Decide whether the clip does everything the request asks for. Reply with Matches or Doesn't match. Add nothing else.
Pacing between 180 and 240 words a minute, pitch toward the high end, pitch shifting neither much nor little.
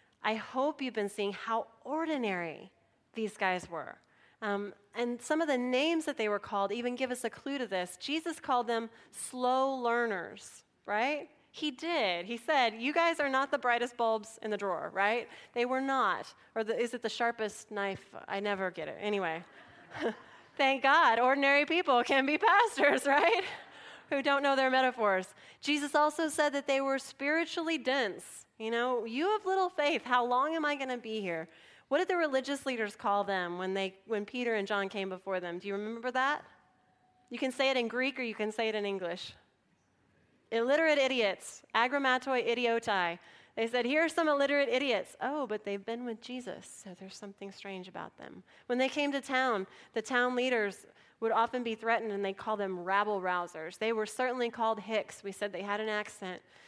Matches